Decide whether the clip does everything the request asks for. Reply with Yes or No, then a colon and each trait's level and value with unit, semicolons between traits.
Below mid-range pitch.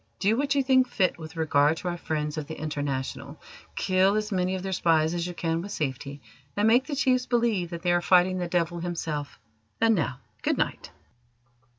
No: medium, 175 Hz